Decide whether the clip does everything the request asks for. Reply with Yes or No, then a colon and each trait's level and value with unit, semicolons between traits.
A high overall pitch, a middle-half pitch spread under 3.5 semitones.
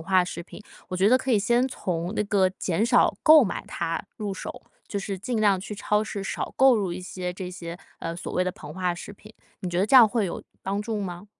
Yes: high, 195 Hz; average, 3.0 semitones